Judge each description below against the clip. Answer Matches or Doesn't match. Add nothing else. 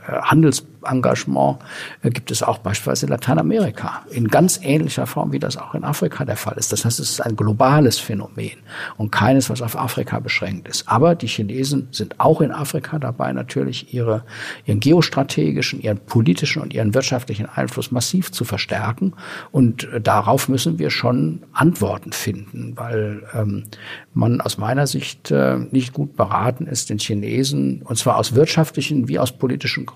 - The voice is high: Doesn't match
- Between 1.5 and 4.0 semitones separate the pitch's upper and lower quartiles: Doesn't match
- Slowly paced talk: Doesn't match